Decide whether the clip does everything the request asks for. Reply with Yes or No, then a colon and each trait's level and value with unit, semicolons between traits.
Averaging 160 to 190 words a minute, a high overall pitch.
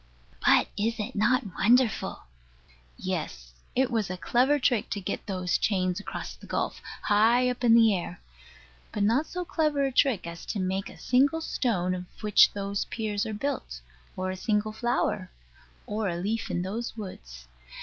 Yes: average, 170 wpm; high, 210 Hz